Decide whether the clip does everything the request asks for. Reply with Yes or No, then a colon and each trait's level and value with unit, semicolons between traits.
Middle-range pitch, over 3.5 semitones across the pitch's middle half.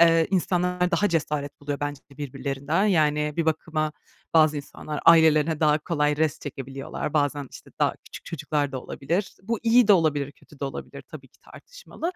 No: medium, 155 Hz; narrow, 2.6 semitones